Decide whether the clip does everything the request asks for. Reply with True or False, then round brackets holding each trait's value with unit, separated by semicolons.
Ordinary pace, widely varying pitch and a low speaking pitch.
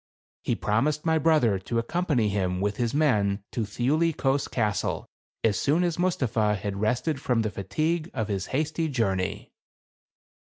True (160 wpm; 6.9 semitones; 120 Hz)